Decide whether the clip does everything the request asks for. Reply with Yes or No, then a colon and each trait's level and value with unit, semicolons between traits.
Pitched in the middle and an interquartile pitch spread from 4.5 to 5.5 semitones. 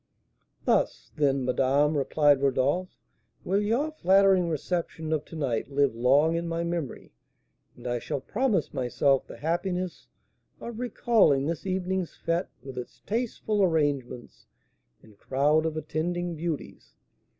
Yes: medium, 160 Hz; average, 4.8 semitones